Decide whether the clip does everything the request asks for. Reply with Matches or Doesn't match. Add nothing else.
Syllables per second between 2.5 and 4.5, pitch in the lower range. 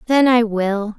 Doesn't match